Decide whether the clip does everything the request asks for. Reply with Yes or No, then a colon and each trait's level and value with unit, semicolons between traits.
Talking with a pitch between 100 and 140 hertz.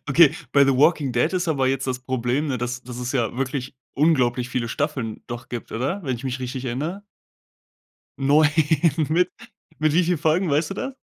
Yes: low, 135 Hz